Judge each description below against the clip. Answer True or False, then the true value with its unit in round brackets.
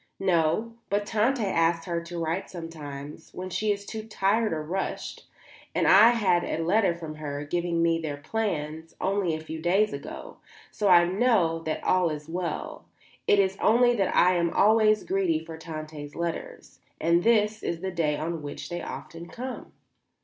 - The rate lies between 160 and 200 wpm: True (180 wpm)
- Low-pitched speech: False (175 Hz)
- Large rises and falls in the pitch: False (4.1 semitones)